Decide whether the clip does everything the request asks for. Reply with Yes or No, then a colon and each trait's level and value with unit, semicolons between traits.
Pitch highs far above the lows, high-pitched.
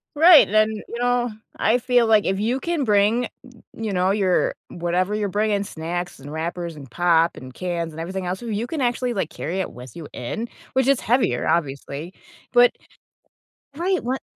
Yes: wide, 6.0 semitones; high, 200 Hz